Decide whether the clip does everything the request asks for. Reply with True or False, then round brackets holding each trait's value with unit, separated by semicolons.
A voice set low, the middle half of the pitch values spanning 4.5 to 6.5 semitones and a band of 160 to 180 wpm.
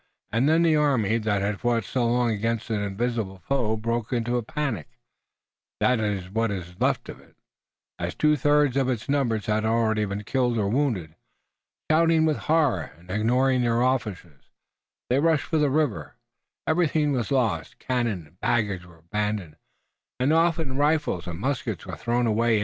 True (115 Hz; 4.9 semitones; 165 wpm)